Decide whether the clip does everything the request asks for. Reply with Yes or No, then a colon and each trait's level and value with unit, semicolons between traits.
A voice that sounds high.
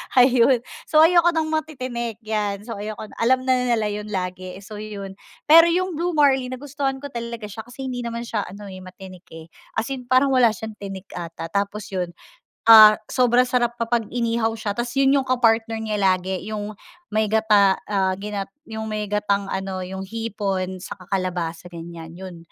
Yes: high, 215 Hz